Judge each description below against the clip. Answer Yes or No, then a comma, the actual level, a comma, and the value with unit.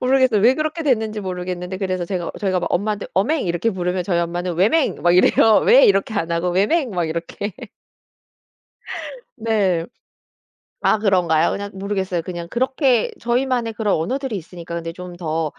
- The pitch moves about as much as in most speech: Yes, average, 4.6 semitones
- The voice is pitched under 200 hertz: Yes, high, 190 Hz